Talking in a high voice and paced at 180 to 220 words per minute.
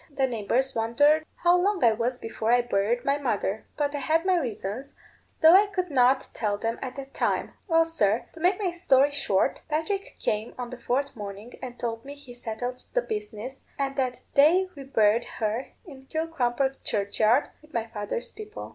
Yes: very high, 265 Hz; average, 190 wpm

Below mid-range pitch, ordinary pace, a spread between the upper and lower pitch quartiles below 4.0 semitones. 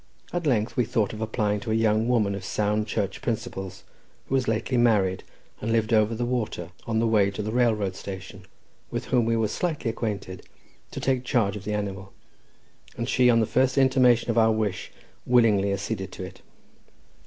Yes: low, 110 Hz; average, 190 wpm; average, 2.9 semitones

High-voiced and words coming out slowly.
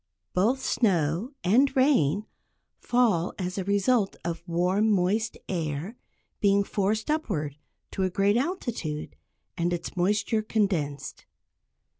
Yes: high, 195 Hz; slow, 115 wpm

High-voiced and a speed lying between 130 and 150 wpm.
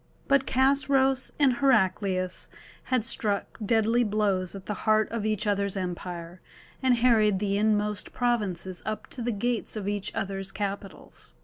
Yes: high, 210 Hz; average, 145 wpm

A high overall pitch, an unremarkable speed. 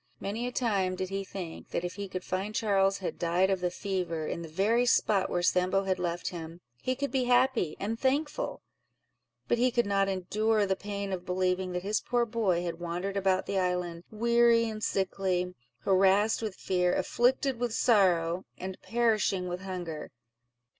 Yes: high, 195 Hz; average, 180 wpm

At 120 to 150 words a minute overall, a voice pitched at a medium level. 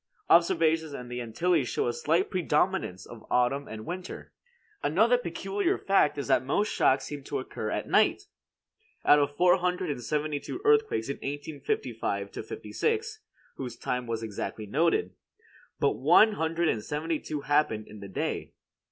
No: average, 160 wpm; medium, 150 Hz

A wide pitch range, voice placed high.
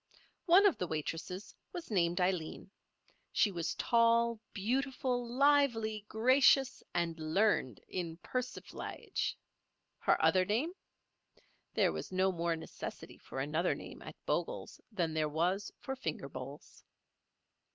Yes: wide, 6.6 semitones; high, 200 Hz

